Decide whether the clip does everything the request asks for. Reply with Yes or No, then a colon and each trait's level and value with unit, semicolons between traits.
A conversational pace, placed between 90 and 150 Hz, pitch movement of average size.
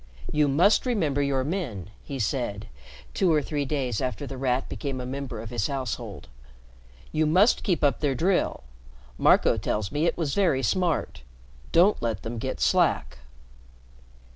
Yes: average, 160 wpm; medium, 140 Hz; average, 4.9 semitones